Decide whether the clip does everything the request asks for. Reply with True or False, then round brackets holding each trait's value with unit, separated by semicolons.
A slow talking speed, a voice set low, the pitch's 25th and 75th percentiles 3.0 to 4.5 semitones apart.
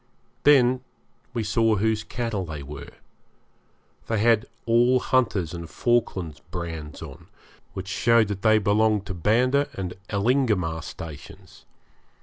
False (125 wpm; 105 Hz; 5.1 semitones)